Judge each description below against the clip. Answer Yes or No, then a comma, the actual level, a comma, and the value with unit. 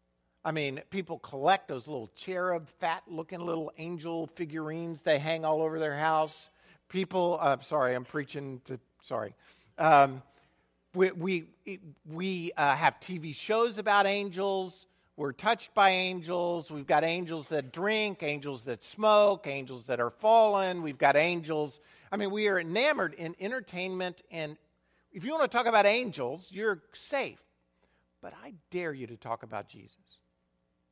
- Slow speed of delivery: No, average, 155 wpm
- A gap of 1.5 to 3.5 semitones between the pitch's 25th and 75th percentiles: No, average, 4.8 semitones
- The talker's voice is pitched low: No, medium, 165 Hz